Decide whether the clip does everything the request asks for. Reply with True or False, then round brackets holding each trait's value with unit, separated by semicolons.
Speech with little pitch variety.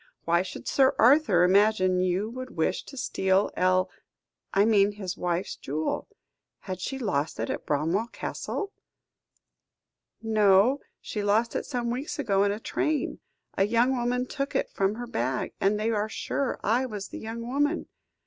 False (4.5 semitones)